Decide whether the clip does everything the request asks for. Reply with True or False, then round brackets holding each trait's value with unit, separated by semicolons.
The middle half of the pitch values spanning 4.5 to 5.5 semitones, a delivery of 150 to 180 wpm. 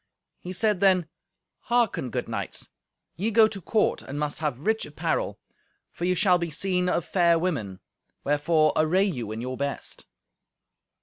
True (4.8 semitones; 160 wpm)